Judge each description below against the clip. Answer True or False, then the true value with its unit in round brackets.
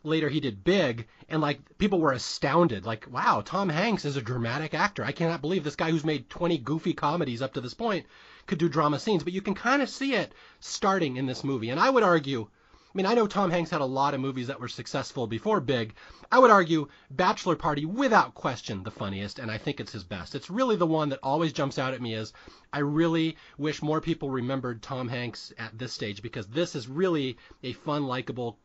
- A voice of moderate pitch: True (145 Hz)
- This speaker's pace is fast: True (230 wpm)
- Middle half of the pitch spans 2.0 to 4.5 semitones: False (5.4 semitones)